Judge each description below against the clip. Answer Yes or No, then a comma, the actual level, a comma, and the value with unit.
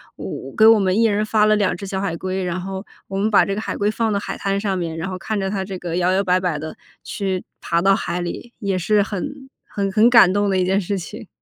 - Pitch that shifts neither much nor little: No, narrow, 2.3 semitones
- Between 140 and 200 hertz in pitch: Yes, high, 195 Hz